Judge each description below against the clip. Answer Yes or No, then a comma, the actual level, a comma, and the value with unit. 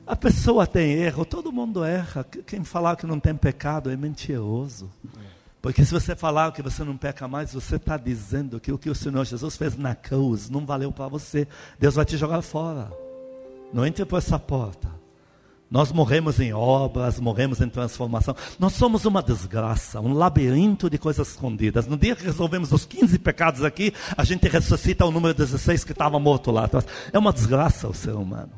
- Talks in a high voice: No, medium, 140 Hz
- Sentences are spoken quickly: Yes, fast, 190 wpm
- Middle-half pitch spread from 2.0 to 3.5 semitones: No, average, 4.6 semitones